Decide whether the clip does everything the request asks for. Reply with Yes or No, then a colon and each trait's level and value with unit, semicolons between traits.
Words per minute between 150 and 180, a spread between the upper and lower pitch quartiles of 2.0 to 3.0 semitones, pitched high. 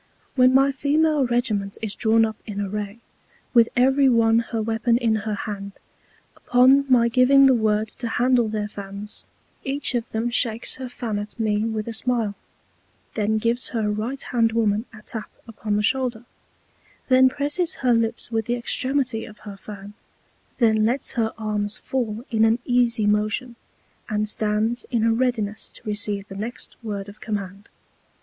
Yes: average, 170 wpm; average, 2.7 semitones; high, 225 Hz